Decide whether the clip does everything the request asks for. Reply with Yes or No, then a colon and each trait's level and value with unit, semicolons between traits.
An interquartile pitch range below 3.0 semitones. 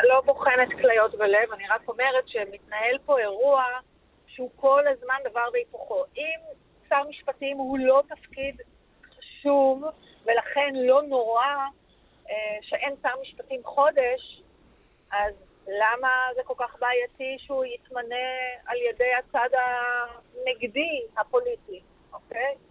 Yes: narrow, 2.4 semitones